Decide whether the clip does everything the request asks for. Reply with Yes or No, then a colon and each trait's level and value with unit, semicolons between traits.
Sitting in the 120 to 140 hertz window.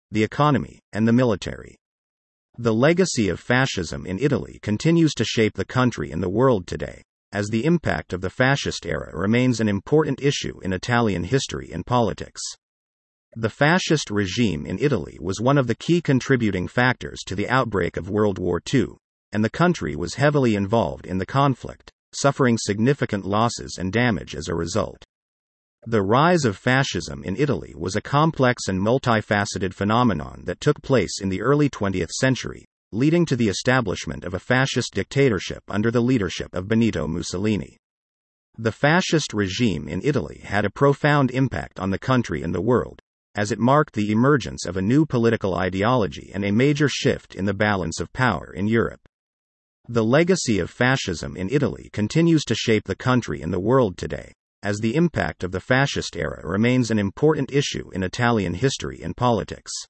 No: low, 110 Hz